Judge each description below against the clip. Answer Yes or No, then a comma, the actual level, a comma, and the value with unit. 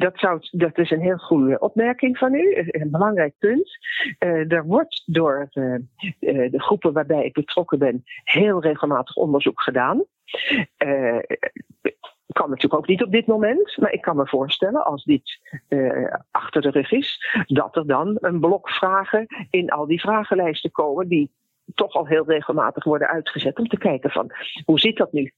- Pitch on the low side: No, medium, 175 Hz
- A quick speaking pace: No, average, 175 wpm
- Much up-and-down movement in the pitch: Yes, wide, 5.9 semitones